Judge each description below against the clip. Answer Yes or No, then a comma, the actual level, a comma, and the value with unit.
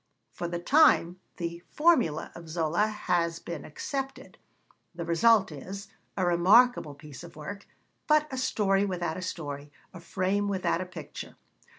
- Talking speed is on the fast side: No, average, 150 wpm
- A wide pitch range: No, average, 3.7 semitones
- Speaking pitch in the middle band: Yes, medium, 180 Hz